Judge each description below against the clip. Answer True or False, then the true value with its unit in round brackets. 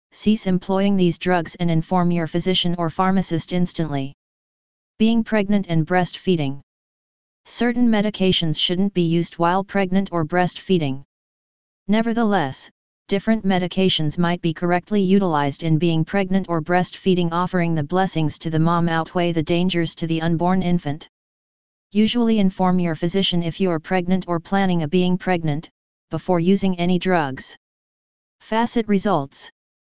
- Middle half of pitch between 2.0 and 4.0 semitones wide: True (2.5 semitones)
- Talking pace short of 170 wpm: True (135 wpm)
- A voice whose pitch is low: False (180 Hz)